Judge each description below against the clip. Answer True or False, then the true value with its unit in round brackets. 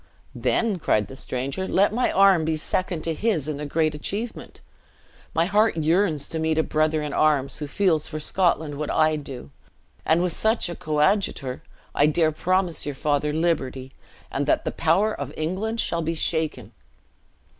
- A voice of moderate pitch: True (160 Hz)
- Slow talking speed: False (175 wpm)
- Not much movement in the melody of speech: False (3.7 semitones)